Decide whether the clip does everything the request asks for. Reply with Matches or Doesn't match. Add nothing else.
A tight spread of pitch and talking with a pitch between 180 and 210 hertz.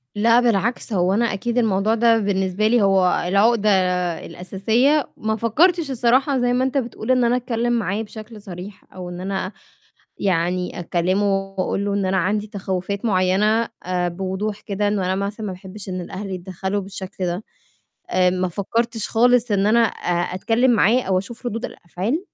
Doesn't match